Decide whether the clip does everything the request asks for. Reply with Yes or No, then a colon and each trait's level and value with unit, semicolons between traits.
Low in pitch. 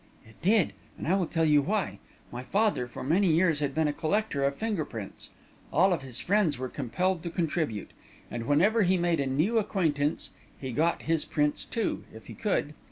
No: medium, 160 Hz